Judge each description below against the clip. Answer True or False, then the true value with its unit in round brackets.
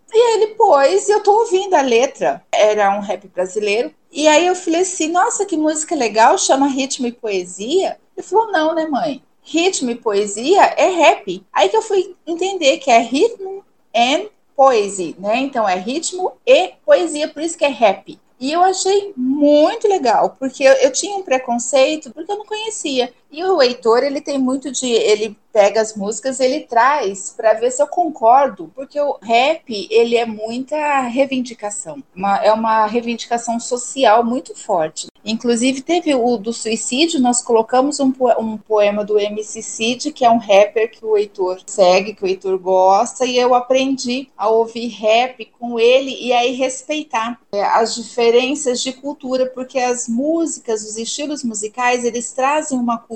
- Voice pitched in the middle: False (255 Hz)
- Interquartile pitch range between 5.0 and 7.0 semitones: True (5.3 semitones)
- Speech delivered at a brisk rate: False (175 wpm)